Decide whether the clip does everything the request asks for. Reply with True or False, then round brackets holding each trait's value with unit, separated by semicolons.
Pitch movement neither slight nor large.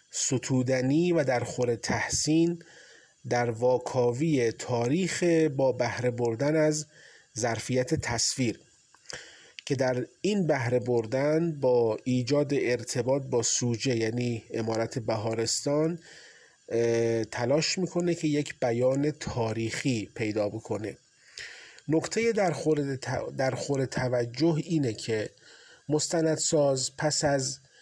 True (4.3 semitones)